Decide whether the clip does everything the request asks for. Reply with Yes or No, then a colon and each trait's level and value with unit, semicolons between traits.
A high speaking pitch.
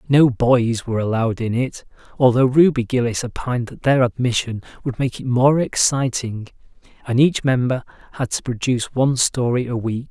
No: low, 125 Hz